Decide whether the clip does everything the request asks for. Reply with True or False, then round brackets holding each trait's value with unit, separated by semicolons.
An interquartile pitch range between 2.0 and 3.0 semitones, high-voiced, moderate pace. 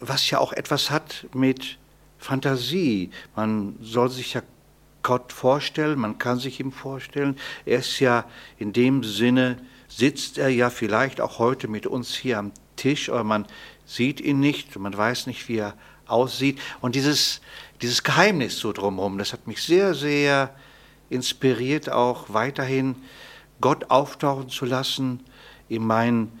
False (2.6 semitones; 125 Hz; 150 wpm)